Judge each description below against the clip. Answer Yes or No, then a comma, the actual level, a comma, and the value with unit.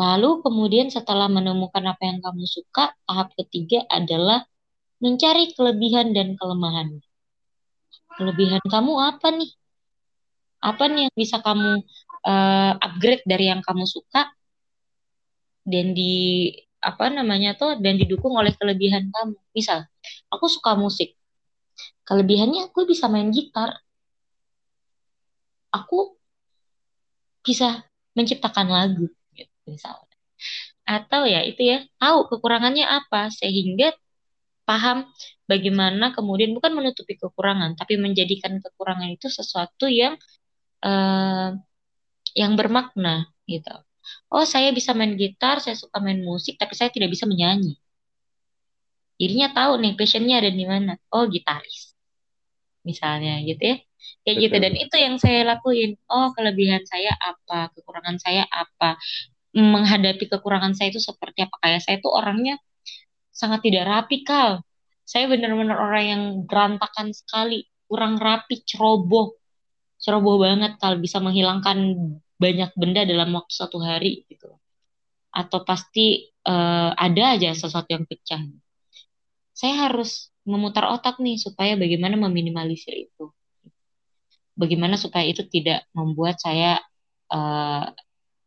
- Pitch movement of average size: Yes, average, 4.5 semitones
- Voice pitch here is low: No, high, 200 Hz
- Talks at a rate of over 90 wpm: Yes, average, 120 wpm